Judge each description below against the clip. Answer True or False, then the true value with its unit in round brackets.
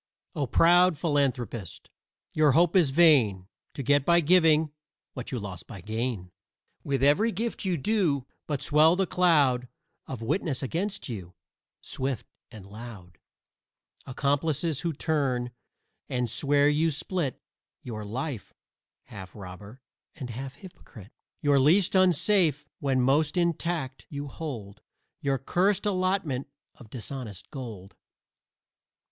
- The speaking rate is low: True (125 wpm)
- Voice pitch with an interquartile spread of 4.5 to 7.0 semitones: True (5.3 semitones)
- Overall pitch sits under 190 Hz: True (140 Hz)